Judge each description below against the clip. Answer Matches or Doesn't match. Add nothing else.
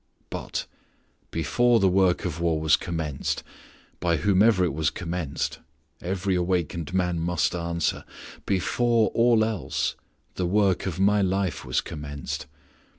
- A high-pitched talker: Doesn't match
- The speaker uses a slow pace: Matches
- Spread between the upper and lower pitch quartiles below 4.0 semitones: Matches